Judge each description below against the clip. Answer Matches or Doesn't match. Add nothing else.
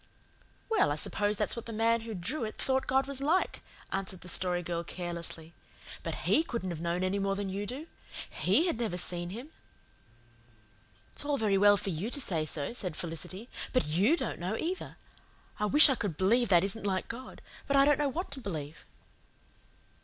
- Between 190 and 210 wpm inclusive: Matches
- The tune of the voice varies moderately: Doesn't match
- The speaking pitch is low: Doesn't match